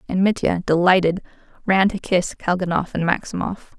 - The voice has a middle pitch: Yes, medium, 180 Hz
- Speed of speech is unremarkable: Yes, average, 145 wpm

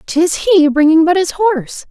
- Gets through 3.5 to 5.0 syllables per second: Yes, 4.9 syllables/s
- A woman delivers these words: Yes, female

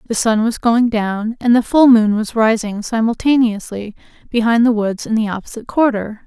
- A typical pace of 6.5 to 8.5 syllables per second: No, 5.1 syllables/s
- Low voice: No, high, 225 Hz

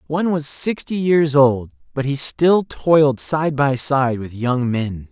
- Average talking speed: Yes, average, 175 wpm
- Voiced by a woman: No, male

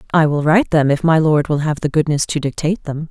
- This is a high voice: No, medium, 155 Hz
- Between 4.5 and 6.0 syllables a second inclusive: No, 6.4 syllables/s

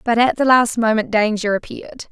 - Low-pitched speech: No, high, 230 Hz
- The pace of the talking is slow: No, average, 200 wpm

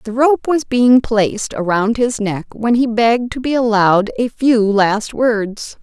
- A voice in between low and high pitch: No, high, 230 Hz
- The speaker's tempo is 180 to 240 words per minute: Yes, average, 185 wpm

